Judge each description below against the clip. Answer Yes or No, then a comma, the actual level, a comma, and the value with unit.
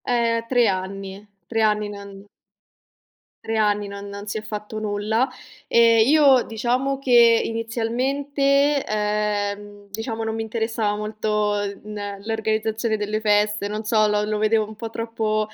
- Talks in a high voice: Yes, high, 215 Hz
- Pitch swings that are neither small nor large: No, narrow, 1.7 semitones